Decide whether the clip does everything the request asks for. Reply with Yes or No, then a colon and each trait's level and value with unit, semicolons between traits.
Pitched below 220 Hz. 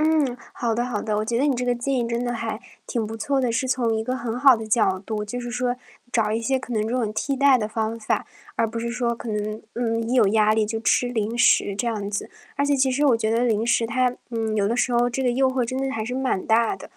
No: high, 235 Hz